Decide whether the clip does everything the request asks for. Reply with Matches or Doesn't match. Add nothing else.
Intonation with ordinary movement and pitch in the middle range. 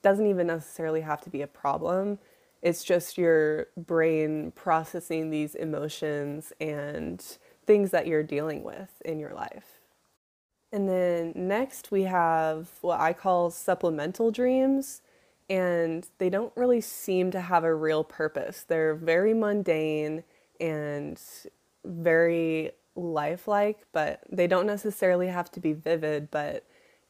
Matches